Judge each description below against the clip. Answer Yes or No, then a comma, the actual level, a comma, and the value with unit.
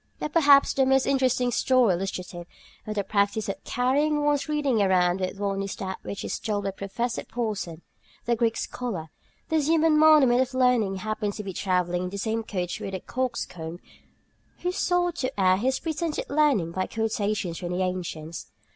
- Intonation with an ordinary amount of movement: No, wide, 6.0 semitones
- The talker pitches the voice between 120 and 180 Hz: No, high, 215 Hz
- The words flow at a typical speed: Yes, average, 180 wpm